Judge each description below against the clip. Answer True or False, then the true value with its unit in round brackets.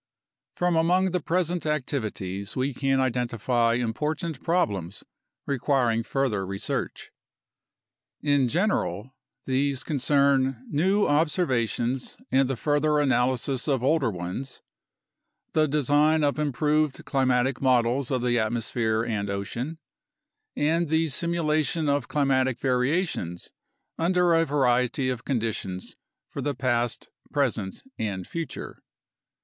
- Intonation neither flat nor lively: True (4.2 semitones)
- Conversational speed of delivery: False (115 wpm)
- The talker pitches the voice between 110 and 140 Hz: True (135 Hz)